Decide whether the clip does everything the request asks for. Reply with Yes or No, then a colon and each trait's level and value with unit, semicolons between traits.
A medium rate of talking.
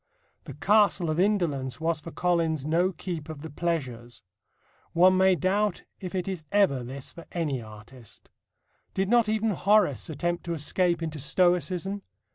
Yes: average, 155 wpm